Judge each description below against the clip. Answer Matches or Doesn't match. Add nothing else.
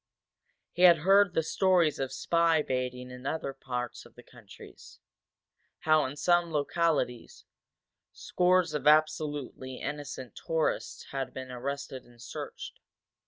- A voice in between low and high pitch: Matches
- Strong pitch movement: Doesn't match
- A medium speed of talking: Doesn't match